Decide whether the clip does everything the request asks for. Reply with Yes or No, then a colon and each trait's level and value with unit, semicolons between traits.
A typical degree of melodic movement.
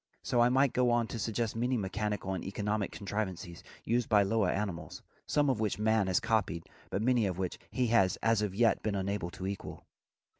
Yes: average, 3.3 semitones